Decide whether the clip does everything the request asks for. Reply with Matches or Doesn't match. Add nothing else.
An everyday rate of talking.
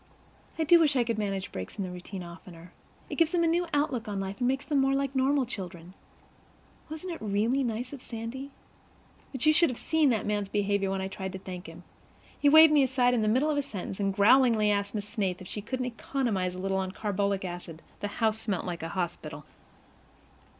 Doesn't match